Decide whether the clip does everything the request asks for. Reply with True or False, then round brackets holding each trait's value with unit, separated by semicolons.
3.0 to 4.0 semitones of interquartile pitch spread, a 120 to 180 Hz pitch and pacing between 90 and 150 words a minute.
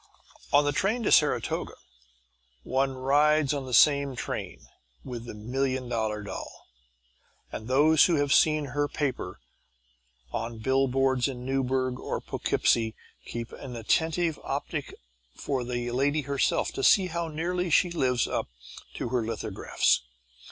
True (3.3 semitones; 135 Hz; 145 wpm)